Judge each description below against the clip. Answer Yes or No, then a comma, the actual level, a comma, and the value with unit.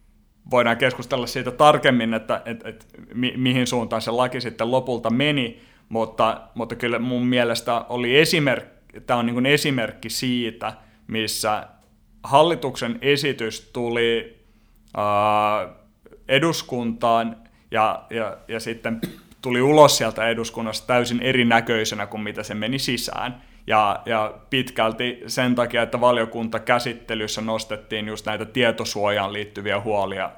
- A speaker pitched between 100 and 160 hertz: Yes, low, 115 Hz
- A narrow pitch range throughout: Yes, narrow, 2.2 semitones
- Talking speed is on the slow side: No, average, 125 wpm